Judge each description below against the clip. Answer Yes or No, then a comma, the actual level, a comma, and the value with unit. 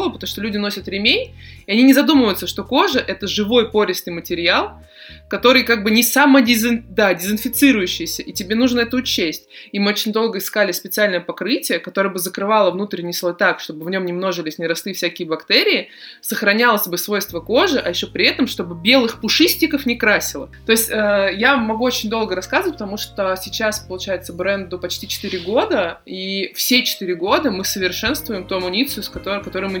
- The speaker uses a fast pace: Yes, fast, 180 wpm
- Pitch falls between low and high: No, high, 205 Hz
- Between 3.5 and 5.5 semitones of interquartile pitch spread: Yes, average, 4.2 semitones